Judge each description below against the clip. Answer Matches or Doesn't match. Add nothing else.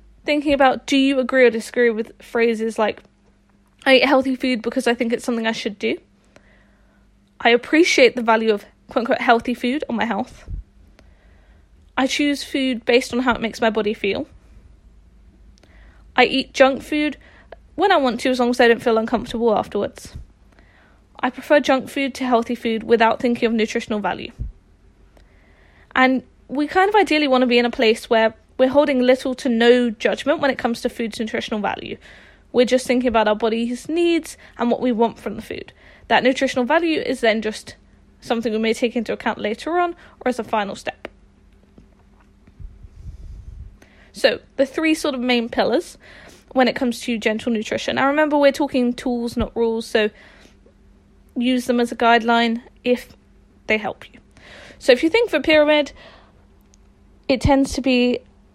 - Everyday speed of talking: Matches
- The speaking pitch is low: Doesn't match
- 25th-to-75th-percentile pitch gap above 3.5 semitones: Doesn't match